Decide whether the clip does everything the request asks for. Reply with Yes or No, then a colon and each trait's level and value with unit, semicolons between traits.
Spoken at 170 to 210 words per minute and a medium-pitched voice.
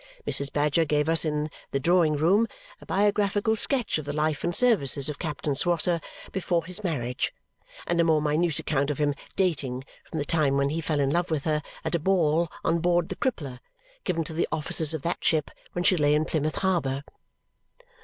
Yes: average, 200 wpm; medium, 160 Hz